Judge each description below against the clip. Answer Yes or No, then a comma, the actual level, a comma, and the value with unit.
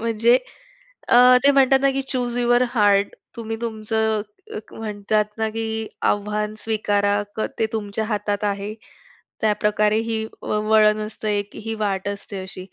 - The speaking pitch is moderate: No, high, 215 Hz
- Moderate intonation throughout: No, narrow, 1.5 semitones